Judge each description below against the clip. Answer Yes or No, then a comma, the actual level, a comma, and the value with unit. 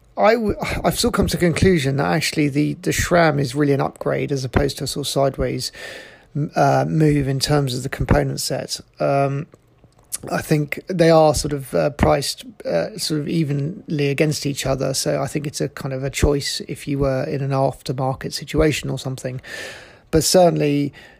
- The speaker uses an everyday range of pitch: No, narrow, 2.1 semitones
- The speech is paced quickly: No, average, 195 wpm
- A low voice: No, medium, 145 Hz